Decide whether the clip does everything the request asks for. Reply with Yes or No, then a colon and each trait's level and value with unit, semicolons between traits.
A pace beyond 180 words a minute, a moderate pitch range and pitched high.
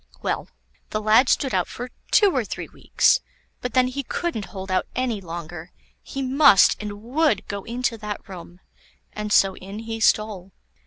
No: average, 170 wpm; average, 4.6 semitones; high, 215 Hz